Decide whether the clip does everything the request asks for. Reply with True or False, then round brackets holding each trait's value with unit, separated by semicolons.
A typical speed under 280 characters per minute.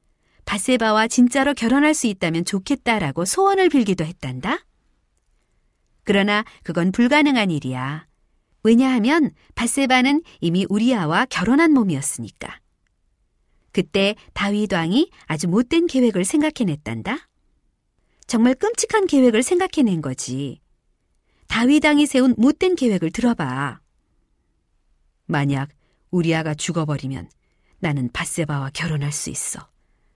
True (265 characters per minute)